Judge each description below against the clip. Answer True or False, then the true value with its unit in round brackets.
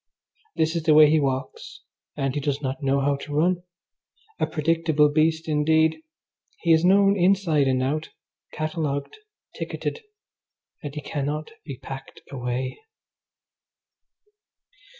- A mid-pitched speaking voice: True (150 Hz)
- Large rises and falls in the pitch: False (2.7 semitones)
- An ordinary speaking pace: False (130 wpm)